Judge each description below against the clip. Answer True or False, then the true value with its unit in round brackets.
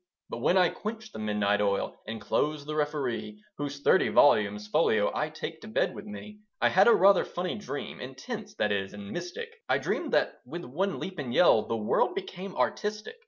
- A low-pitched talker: False (155 Hz)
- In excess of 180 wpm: True (200 wpm)